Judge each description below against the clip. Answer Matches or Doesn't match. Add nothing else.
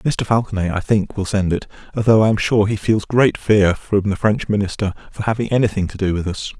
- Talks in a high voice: Doesn't match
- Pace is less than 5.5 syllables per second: Doesn't match